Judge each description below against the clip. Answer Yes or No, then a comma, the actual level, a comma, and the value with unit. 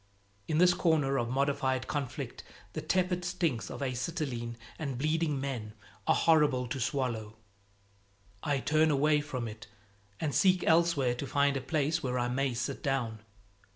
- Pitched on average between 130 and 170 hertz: Yes, medium, 140 Hz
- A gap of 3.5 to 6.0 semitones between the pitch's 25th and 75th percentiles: Yes, average, 3.8 semitones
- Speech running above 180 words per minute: No, average, 155 wpm